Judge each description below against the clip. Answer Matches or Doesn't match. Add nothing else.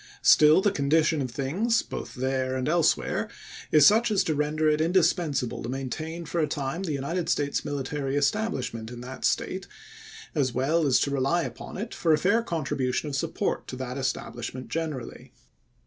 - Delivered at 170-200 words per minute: Matches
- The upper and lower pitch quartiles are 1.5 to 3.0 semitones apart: Doesn't match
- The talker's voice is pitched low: Doesn't match